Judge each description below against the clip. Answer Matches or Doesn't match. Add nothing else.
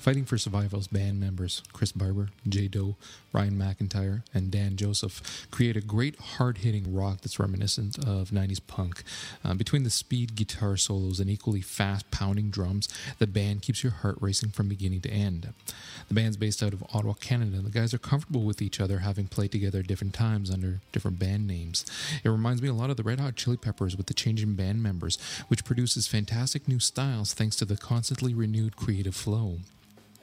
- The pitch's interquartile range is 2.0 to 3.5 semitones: Matches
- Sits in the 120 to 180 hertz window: Doesn't match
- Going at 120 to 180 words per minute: Doesn't match